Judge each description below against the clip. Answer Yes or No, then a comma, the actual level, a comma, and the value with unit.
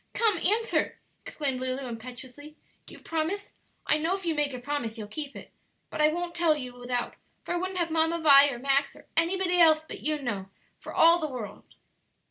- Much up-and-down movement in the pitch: No, average, 4.8 semitones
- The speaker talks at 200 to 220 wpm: Yes, fast, 205 wpm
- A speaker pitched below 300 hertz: No, very high, 305 Hz